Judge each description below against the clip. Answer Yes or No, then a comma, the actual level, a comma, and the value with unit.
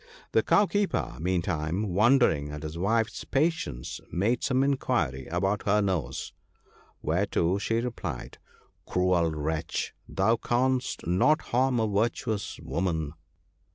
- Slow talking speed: Yes, slow, 120 wpm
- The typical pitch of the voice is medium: No, low, 100 Hz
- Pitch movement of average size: No, wide, 6.5 semitones